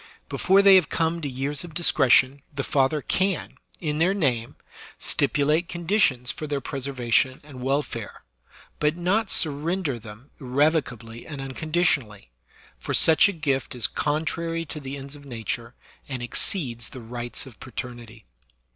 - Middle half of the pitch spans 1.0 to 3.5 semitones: No, average, 4.6 semitones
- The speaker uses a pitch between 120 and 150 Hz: Yes, medium, 140 Hz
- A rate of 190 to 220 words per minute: No, average, 145 wpm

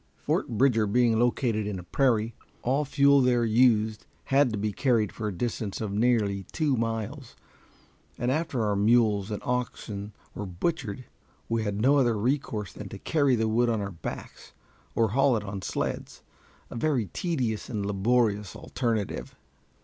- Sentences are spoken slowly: No, average, 165 wpm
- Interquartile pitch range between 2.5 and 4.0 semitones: Yes, average, 3.3 semitones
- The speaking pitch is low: Yes, low, 115 Hz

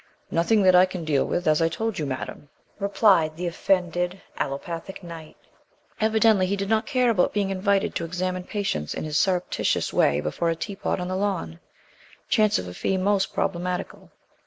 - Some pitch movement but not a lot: Yes, average, 3.2 semitones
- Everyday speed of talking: Yes, average, 180 wpm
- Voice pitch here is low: No, medium, 185 Hz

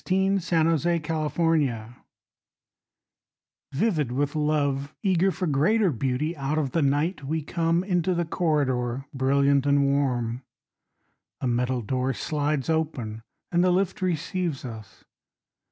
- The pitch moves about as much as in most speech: Yes, average, 4.1 semitones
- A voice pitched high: No, medium, 150 Hz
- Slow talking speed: Yes, slow, 125 wpm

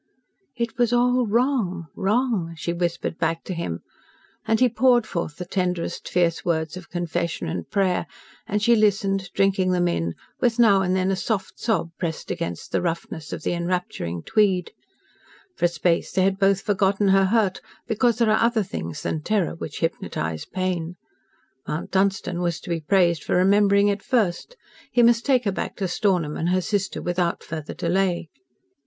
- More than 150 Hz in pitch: Yes, medium, 185 Hz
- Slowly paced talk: No, average, 175 wpm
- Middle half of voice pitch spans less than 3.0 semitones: No, average, 3.6 semitones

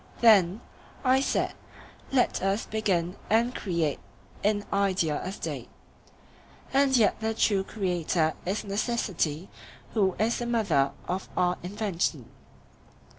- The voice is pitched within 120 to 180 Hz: No, high, 200 Hz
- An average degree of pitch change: Yes, average, 3.9 semitones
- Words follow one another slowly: Yes, slow, 120 wpm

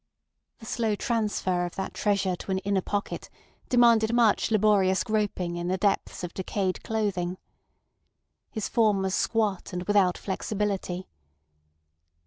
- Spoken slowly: Yes, slow, 130 wpm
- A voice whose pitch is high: Yes, high, 200 Hz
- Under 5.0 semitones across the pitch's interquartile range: Yes, narrow, 2.6 semitones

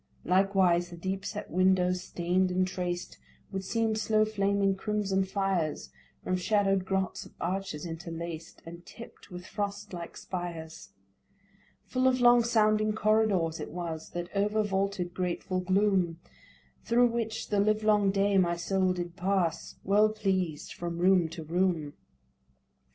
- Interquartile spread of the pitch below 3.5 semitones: Yes, average, 2.9 semitones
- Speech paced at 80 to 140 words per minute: Yes, slow, 135 wpm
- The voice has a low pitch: No, high, 190 Hz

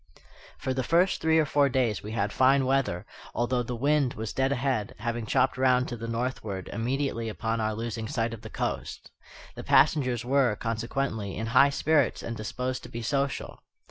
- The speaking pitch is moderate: No, low, 120 Hz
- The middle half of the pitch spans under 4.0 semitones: Yes, average, 3.3 semitones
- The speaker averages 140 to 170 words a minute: No, average, 185 wpm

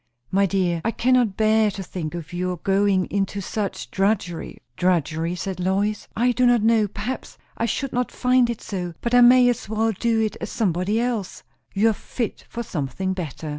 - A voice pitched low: No, high, 205 Hz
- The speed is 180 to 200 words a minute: Yes, average, 190 wpm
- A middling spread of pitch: Yes, average, 4.0 semitones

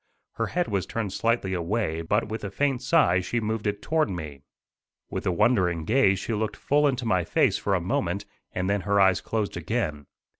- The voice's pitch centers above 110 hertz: No, low, 105 Hz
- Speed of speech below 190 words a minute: No, average, 200 wpm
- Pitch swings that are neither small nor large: Yes, average, 4.2 semitones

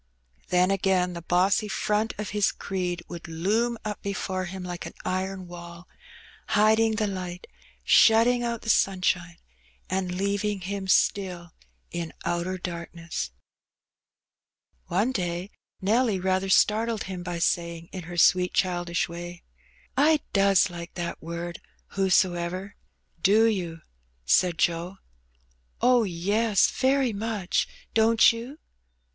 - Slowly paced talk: Yes, slow, 130 wpm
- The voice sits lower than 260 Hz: Yes, medium, 185 Hz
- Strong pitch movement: No, average, 3.2 semitones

